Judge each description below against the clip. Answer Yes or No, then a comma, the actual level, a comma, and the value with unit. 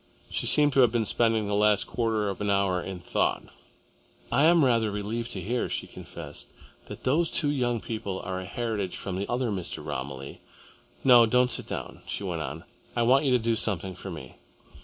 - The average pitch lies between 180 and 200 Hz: No, low, 110 Hz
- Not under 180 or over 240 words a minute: Yes, average, 200 wpm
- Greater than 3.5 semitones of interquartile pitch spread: Yes, average, 4.2 semitones